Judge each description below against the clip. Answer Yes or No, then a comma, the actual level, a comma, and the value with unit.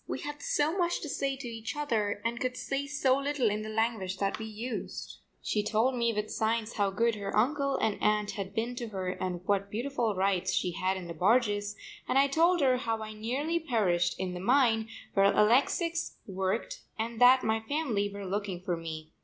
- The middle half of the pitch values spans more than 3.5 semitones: Yes, average, 4.6 semitones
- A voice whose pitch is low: No, high, 220 Hz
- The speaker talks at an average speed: No, fast, 210 wpm